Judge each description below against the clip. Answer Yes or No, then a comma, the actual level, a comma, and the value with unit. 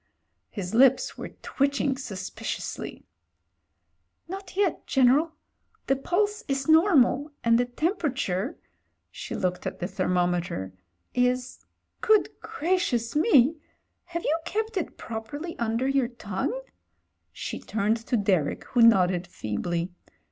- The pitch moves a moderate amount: No, wide, 8.4 semitones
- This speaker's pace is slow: Yes, slow, 125 wpm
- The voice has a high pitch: Yes, very high, 250 Hz